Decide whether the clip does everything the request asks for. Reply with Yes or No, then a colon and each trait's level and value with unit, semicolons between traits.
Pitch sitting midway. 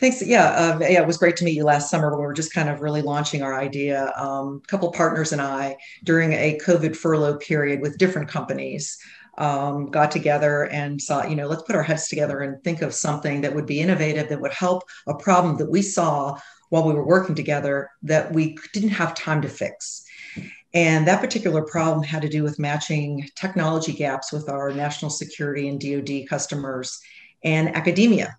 Yes: medium, 150 Hz